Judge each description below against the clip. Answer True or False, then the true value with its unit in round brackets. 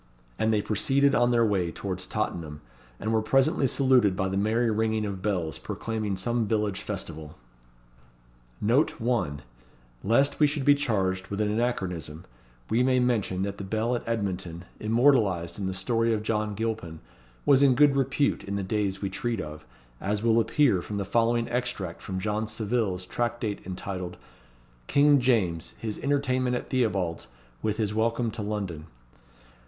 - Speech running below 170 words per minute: True (160 wpm)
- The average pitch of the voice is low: True (110 Hz)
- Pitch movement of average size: True (4.0 semitones)